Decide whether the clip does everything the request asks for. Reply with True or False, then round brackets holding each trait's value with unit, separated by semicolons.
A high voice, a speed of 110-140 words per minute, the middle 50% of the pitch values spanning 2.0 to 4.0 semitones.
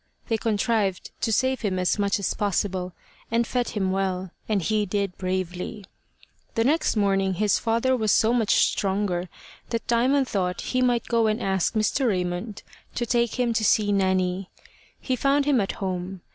False (205 Hz; 175 wpm; 3.7 semitones)